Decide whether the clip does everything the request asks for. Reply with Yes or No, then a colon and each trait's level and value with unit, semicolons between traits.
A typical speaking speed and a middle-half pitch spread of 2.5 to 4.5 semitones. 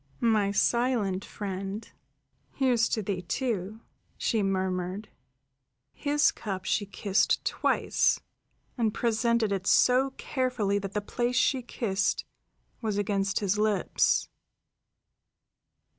No: slow, 105 wpm; average, 3.1 semitones